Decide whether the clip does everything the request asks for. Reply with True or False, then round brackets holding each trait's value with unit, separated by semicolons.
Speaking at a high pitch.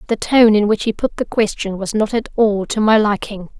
True (215 Hz)